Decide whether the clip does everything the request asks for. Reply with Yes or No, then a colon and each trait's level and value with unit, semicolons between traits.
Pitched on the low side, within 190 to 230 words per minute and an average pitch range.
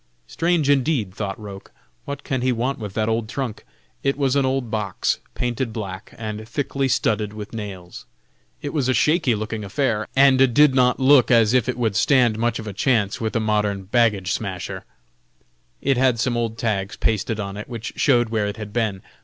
Yes: low, 115 Hz; average, 195 wpm; average, 3.8 semitones